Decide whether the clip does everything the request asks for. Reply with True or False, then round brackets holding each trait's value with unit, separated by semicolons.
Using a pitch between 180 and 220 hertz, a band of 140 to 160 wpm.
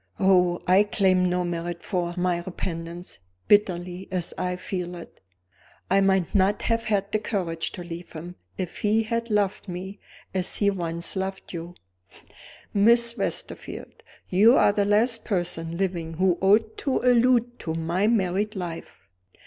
True (190 Hz; 150 wpm)